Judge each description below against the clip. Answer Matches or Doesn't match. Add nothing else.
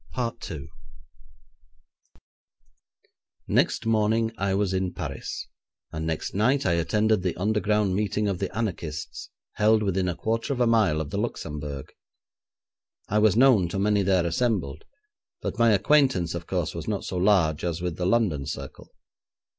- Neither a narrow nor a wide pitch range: Matches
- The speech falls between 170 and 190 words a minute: Doesn't match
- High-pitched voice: Doesn't match